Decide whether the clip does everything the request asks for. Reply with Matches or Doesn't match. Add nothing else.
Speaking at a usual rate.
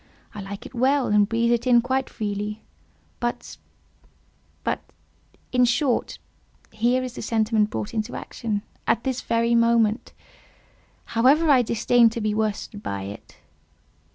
Doesn't match